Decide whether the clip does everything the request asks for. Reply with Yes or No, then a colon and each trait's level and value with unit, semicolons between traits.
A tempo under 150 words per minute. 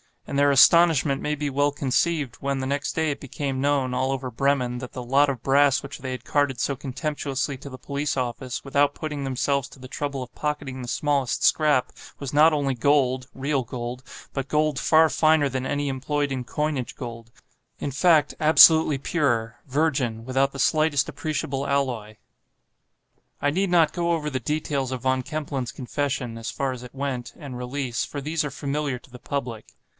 No: average, 180 wpm